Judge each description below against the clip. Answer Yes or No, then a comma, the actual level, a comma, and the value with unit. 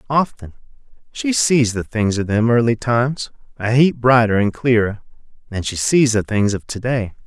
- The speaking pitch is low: Yes, low, 115 Hz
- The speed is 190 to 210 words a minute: No, average, 175 wpm